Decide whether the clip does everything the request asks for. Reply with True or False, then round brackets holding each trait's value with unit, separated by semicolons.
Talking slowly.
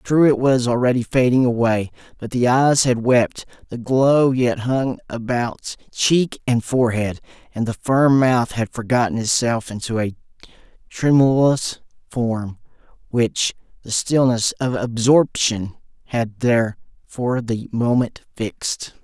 True (130 wpm)